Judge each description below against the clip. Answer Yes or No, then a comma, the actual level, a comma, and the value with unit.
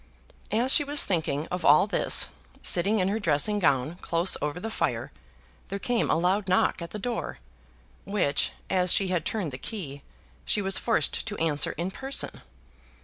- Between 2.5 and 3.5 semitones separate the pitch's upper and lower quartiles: No, average, 4.4 semitones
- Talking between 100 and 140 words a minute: No, average, 175 wpm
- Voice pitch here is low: No, medium, 185 Hz